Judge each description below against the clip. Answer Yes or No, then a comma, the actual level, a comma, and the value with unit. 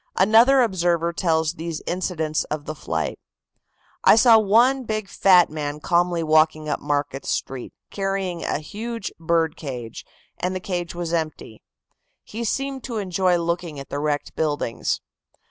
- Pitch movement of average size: Yes, average, 4.2 semitones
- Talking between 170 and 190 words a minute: No, average, 145 wpm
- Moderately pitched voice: Yes, medium, 170 Hz